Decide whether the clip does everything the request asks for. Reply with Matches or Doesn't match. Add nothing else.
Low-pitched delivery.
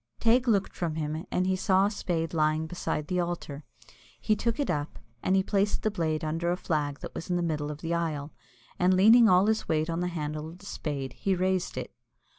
Doesn't match